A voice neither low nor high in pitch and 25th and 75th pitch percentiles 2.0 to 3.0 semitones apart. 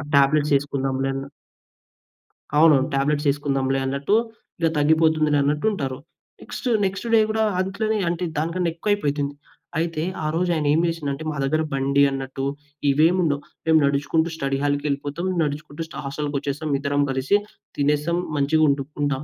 Yes: medium, 145 Hz; narrow, 2.6 semitones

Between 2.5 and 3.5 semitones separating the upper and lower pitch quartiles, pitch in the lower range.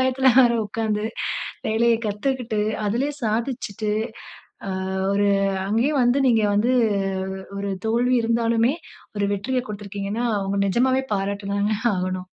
No: average, 3.2 semitones; high, 220 Hz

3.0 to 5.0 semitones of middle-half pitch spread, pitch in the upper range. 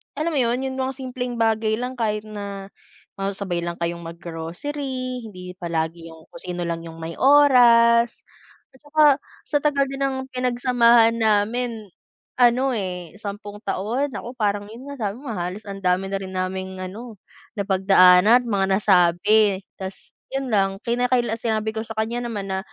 Yes: average, 4.7 semitones; high, 215 Hz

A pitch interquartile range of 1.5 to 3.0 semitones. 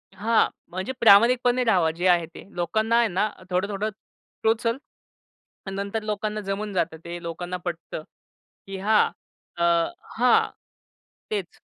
No: average, 3.8 semitones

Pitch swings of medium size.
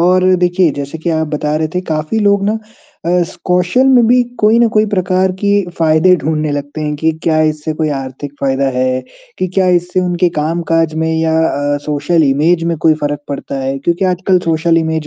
Yes: average, 3.4 semitones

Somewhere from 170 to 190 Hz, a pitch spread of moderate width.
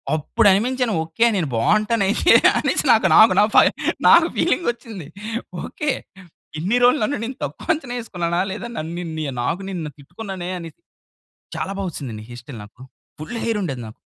No: medium, 185 Hz; wide, 6.6 semitones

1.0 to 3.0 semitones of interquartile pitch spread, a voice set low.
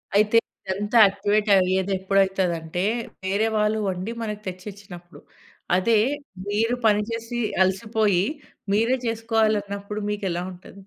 No: narrow, 2.5 semitones; high, 205 Hz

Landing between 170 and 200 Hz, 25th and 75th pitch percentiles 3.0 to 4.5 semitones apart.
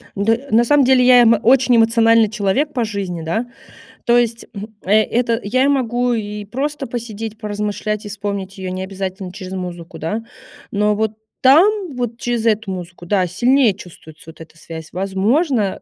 No: high, 215 Hz; average, 4.0 semitones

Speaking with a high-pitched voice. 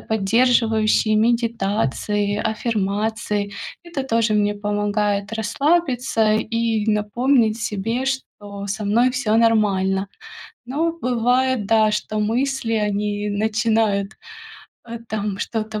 Yes: high, 220 Hz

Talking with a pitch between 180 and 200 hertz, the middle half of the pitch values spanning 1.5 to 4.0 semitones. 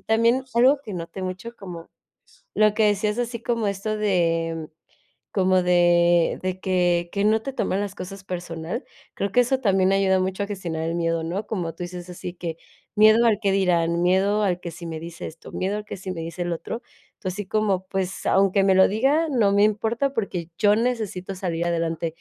Yes: high, 190 Hz; average, 3.4 semitones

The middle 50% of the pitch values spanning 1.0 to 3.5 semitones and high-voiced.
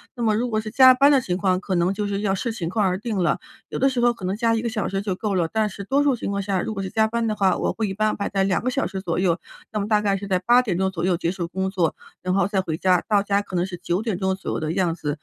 Yes: average, 3.0 semitones; high, 200 Hz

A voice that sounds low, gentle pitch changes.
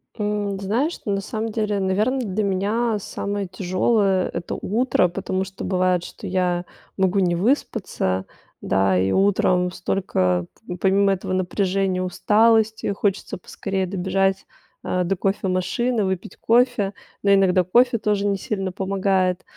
No: high, 195 Hz; narrow, 2.2 semitones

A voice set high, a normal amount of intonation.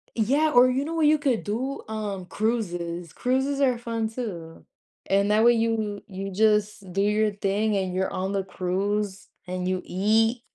Yes: high, 210 Hz; average, 3.5 semitones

